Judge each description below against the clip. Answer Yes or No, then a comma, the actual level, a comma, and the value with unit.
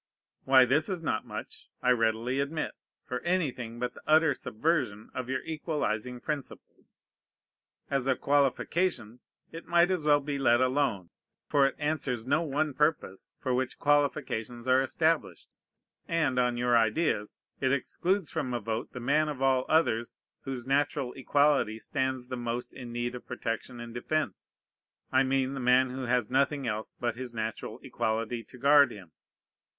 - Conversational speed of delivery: Yes, average, 160 wpm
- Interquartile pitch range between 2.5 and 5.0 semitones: Yes, average, 3.4 semitones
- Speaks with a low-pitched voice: Yes, low, 130 Hz